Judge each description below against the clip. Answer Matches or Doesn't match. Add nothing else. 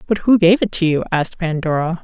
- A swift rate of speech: Matches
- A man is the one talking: Doesn't match